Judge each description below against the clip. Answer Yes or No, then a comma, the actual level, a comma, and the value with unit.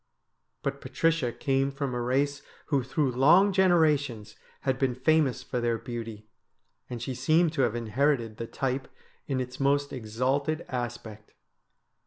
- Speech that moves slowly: No, average, 145 wpm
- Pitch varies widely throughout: No, average, 3.2 semitones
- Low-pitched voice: Yes, low, 130 Hz